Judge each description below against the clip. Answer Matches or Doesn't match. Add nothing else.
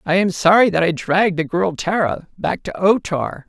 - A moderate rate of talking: Doesn't match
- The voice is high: Doesn't match